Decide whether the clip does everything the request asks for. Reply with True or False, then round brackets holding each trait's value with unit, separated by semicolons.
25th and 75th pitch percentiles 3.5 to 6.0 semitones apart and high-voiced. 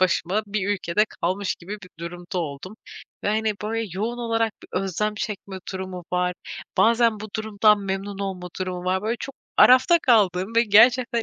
False (3.1 semitones; 205 Hz)